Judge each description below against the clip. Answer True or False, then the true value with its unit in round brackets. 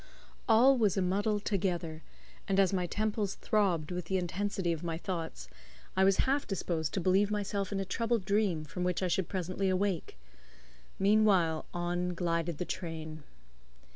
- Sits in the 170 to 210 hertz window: True (185 Hz)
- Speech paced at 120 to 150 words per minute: False (165 wpm)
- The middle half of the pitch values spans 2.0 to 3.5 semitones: True (3.0 semitones)